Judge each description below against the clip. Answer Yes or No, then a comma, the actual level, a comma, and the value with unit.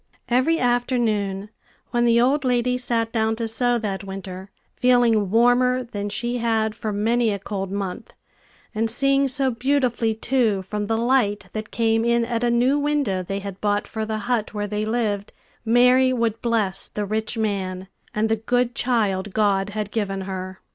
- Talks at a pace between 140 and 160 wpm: No, average, 175 wpm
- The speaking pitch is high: Yes, high, 225 Hz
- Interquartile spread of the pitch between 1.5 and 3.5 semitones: Yes, average, 3.0 semitones